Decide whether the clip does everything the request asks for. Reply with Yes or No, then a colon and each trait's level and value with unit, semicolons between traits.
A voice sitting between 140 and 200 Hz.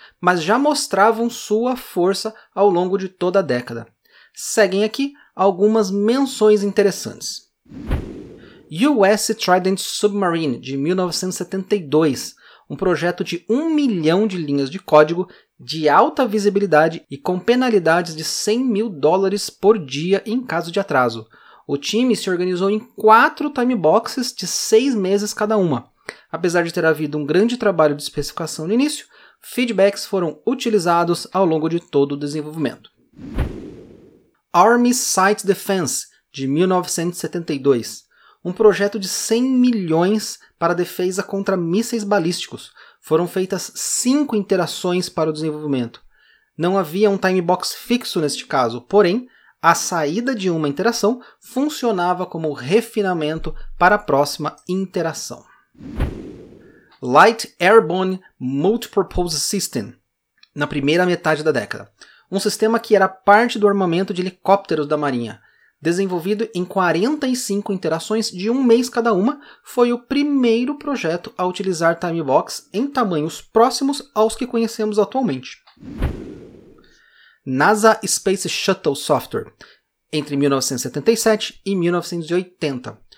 Yes: high, 190 Hz